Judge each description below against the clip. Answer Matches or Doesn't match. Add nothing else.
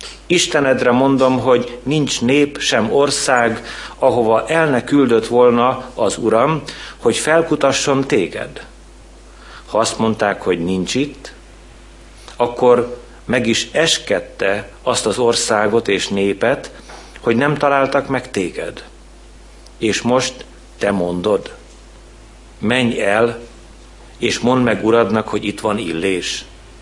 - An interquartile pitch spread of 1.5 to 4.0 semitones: Matches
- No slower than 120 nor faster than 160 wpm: Doesn't match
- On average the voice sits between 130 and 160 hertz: Doesn't match